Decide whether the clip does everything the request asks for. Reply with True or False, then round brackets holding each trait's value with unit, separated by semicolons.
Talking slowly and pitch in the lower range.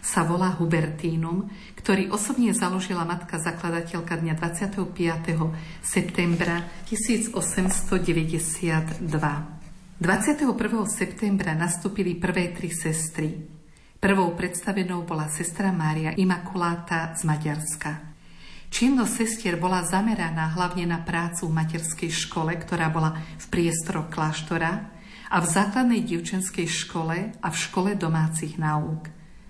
False (105 wpm; 170 Hz)